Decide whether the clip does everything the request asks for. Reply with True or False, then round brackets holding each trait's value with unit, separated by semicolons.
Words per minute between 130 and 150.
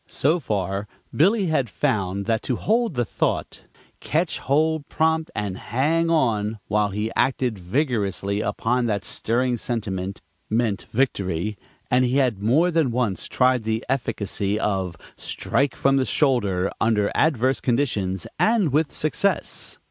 True (140 wpm)